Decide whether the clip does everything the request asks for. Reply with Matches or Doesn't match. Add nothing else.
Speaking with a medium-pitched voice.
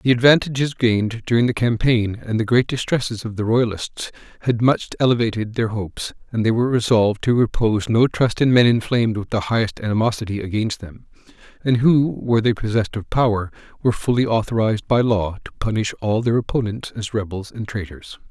Doesn't match